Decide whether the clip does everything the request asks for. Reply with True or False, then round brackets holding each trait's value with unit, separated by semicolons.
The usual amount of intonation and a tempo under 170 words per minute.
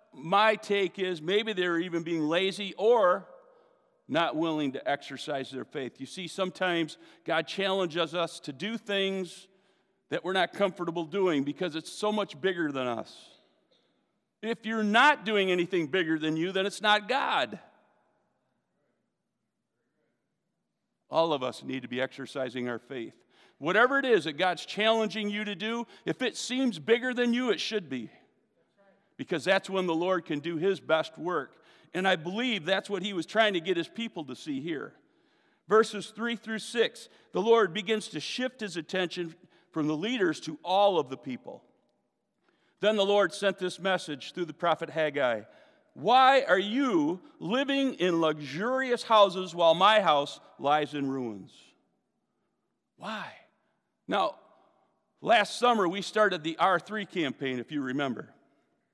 True (4.9 semitones; 155 wpm)